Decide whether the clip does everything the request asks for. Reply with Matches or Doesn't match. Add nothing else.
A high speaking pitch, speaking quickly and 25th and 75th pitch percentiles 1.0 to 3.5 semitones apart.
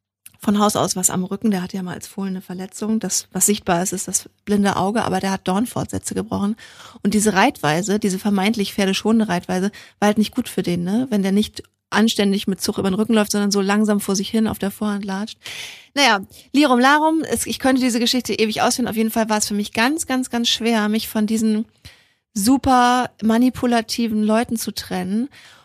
Matches